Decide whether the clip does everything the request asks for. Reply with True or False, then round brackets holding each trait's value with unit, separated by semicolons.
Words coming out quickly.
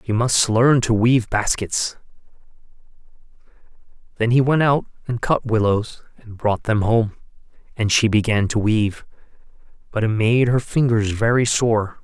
False (145 wpm)